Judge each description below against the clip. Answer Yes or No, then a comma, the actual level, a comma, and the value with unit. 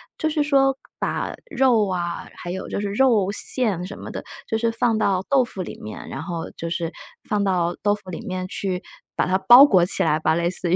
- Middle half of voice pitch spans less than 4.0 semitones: No, average, 4.7 semitones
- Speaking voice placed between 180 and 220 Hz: Yes, high, 195 Hz